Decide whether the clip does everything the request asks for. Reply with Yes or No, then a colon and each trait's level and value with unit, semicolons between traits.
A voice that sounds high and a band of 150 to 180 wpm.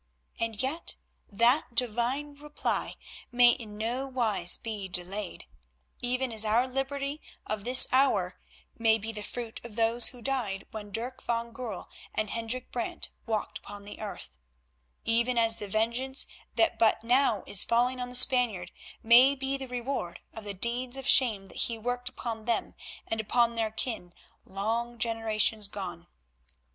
Yes: high, 230 Hz; average, 155 wpm